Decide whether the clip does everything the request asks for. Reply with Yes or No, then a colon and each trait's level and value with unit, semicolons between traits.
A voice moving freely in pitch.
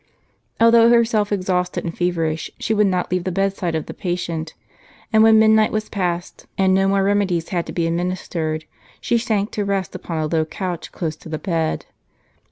No: average, 3.5 semitones